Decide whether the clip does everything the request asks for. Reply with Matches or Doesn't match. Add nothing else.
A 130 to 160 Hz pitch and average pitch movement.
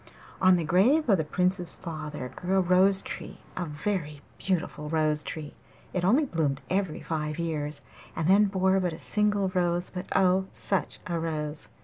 Doesn't match